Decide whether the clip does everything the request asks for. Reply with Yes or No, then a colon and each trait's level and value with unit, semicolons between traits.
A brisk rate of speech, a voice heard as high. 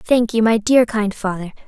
Yes: fast, 215 wpm; high, 220 Hz